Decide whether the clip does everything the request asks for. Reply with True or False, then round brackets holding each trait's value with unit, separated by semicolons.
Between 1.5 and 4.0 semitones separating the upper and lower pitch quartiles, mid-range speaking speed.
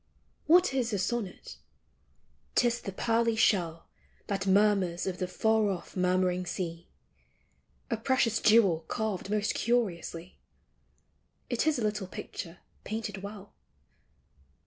False (3.6 semitones; 125 wpm)